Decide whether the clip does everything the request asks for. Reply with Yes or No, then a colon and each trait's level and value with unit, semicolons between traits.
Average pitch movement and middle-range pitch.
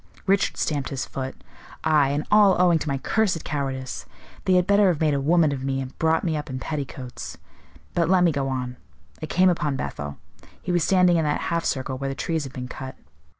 Yes: average, 4.4 semitones; medium, 150 Hz